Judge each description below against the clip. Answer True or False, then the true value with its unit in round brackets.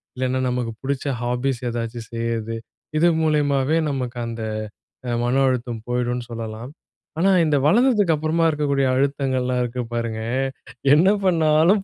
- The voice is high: False (130 Hz)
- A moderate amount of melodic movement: True (4.1 semitones)